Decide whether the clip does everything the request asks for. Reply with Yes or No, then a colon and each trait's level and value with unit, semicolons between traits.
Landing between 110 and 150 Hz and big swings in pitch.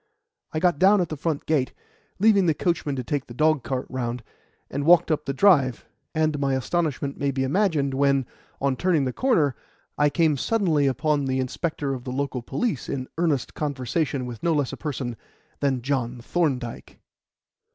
No: medium, 140 Hz; average, 3.5 semitones